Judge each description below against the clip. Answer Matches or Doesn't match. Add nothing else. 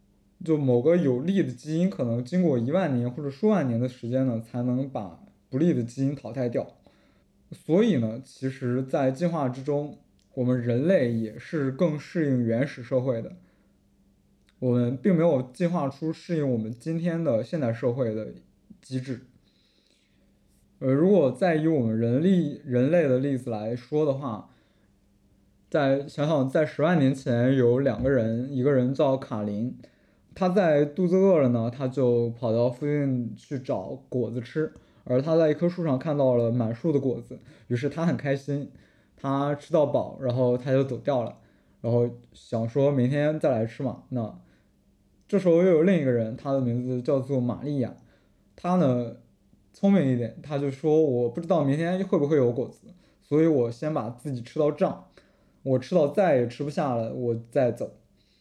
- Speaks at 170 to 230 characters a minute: Doesn't match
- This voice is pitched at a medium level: Doesn't match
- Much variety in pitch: Doesn't match